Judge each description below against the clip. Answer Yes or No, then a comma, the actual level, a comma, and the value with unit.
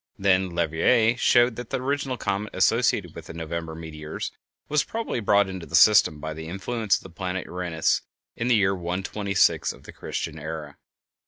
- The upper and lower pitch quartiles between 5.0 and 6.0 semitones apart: Yes, wide, 5.5 semitones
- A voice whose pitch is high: No, very low, 95 Hz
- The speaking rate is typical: Yes, average, 175 wpm